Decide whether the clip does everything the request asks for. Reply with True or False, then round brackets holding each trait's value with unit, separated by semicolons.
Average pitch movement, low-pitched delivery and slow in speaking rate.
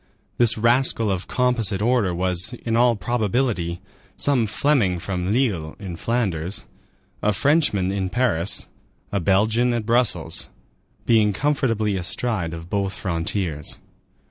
True (4.8 semitones; 105 Hz; 120 wpm)